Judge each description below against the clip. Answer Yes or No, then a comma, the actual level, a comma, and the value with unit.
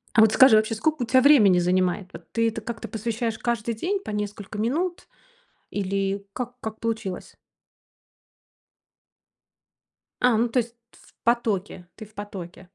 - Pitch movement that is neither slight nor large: Yes, average, 3.0 semitones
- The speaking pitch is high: Yes, high, 220 Hz